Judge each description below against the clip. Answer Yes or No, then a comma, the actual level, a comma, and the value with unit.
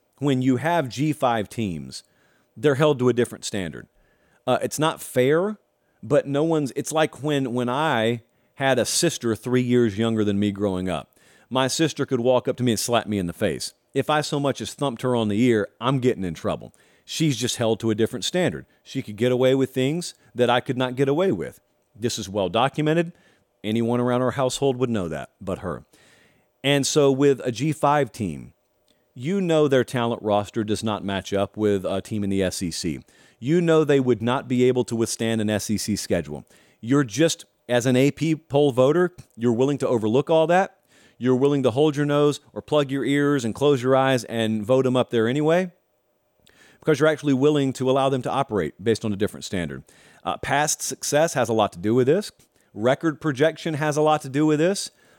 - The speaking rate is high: Yes, fast, 210 wpm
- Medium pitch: No, low, 130 Hz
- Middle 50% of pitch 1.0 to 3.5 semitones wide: No, average, 4.3 semitones